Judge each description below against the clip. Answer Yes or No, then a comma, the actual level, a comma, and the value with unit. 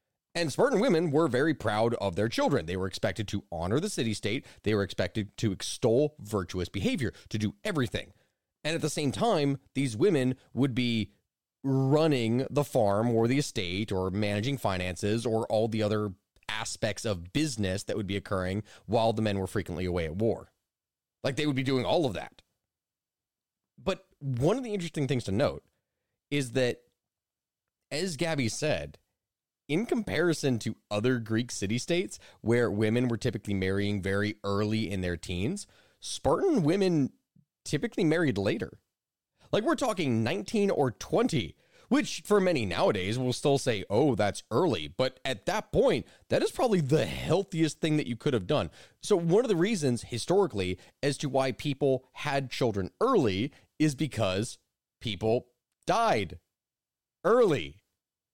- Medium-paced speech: Yes, average, 160 wpm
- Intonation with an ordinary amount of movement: No, wide, 5.7 semitones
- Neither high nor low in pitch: No, low, 115 Hz